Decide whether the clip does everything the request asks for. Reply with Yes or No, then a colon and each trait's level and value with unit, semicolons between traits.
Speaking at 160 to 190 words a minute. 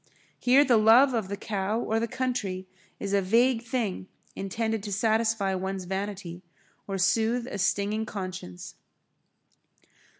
No: slow, 135 wpm